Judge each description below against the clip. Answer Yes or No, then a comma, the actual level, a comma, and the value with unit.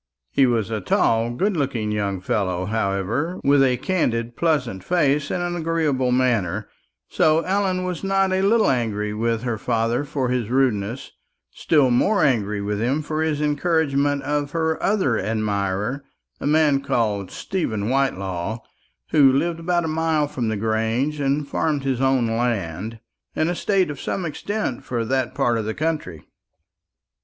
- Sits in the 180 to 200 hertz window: No, low, 135 Hz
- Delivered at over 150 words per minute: Yes, average, 160 wpm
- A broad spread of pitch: Yes, wide, 5.9 semitones